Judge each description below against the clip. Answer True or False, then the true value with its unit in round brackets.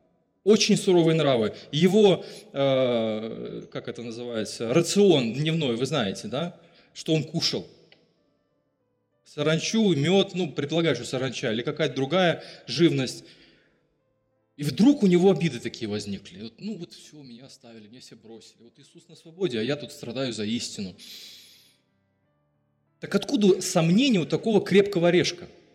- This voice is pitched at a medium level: True (150 Hz)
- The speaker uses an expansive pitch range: True (7.3 semitones)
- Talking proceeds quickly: False (135 wpm)